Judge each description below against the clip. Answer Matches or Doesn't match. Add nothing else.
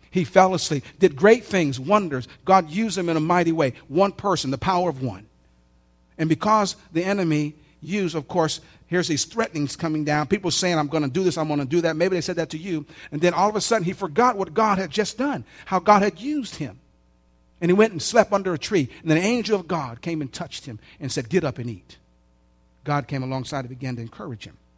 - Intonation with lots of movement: Matches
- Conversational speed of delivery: Doesn't match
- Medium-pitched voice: Matches